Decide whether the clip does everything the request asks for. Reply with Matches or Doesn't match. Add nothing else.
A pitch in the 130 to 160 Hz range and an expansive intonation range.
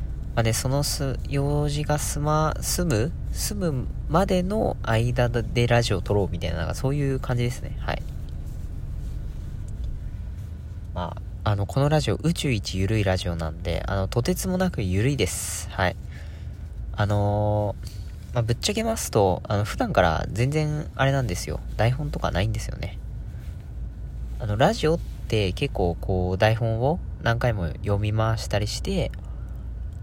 Doesn't match